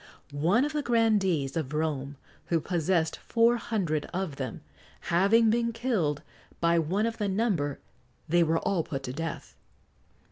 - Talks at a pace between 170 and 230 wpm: No, average, 150 wpm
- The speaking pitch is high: No, medium, 175 Hz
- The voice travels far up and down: Yes, wide, 6.6 semitones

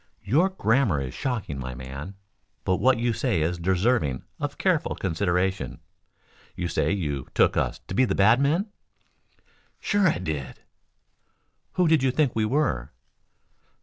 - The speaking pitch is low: Yes, low, 100 Hz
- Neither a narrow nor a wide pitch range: No, wide, 9.0 semitones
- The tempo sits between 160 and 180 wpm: No, average, 145 wpm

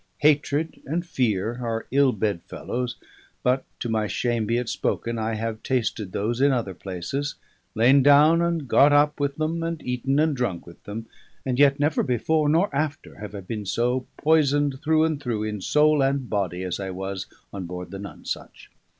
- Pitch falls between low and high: No, low, 125 Hz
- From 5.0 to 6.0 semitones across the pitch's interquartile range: Yes, average, 5.3 semitones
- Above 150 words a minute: Yes, average, 185 wpm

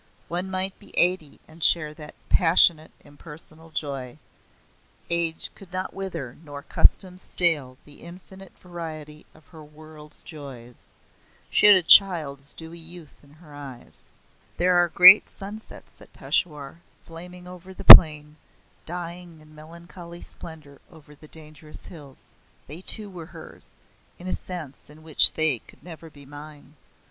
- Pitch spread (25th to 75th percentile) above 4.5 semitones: No, average, 2.9 semitones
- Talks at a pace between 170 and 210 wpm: No, average, 145 wpm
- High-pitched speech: No, medium, 160 Hz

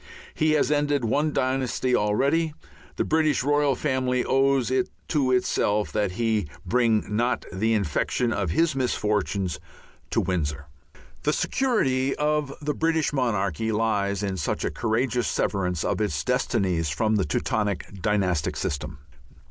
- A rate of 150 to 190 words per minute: No, average, 140 wpm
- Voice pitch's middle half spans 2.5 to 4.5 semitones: No, average, 5.3 semitones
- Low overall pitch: Yes, low, 115 Hz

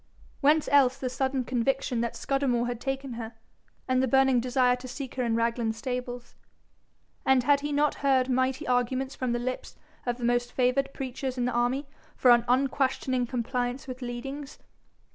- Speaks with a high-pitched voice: Yes, very high, 255 Hz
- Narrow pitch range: Yes, narrow, 1.7 semitones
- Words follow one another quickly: No, average, 175 wpm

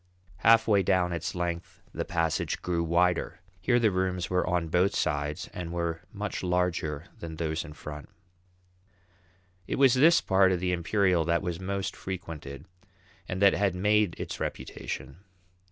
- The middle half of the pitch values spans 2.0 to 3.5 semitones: Yes, narrow, 2.5 semitones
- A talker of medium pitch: No, very low, 90 Hz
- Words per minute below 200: Yes, average, 155 wpm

